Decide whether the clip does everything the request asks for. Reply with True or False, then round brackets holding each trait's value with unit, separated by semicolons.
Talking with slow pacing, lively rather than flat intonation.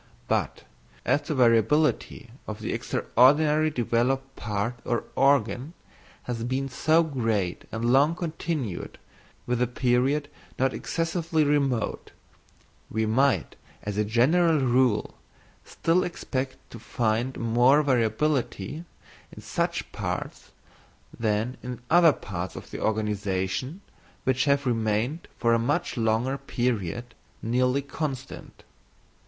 False (115 wpm; 4.1 semitones)